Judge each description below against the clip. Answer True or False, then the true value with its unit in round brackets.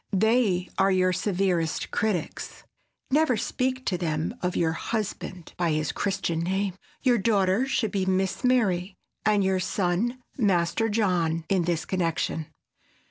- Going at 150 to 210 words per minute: False (135 wpm)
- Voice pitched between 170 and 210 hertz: True (190 Hz)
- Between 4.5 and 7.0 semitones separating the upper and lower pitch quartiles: False (3.4 semitones)